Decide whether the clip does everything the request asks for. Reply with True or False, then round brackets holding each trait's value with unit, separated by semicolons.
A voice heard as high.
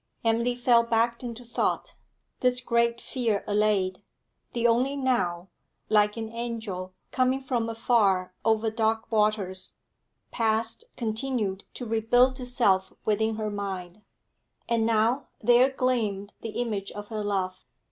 True (225 Hz)